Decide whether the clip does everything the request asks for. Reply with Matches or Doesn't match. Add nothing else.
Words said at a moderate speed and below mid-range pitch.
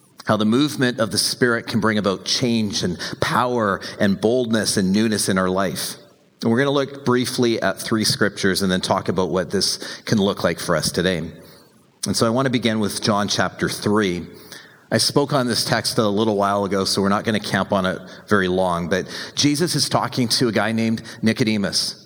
Doesn't match